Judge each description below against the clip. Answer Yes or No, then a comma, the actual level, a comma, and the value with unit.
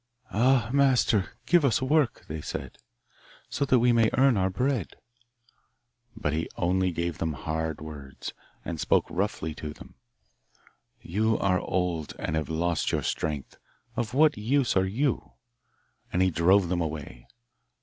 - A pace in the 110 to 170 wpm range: Yes, average, 150 wpm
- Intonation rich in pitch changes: Yes, wide, 7.0 semitones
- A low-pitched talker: Yes, very low, 95 Hz